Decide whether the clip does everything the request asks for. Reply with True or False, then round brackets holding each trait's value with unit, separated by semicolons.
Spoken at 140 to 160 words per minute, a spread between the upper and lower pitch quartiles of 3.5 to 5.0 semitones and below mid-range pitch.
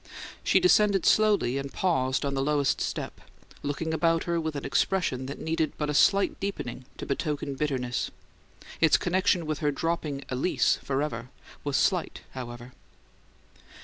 False (145 wpm; 3.9 semitones; 150 Hz)